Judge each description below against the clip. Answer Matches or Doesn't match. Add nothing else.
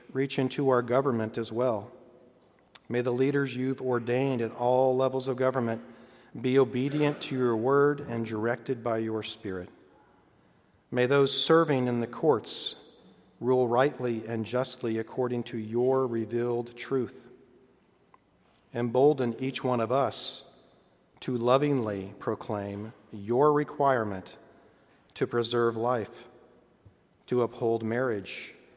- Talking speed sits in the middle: Doesn't match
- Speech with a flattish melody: Matches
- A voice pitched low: Matches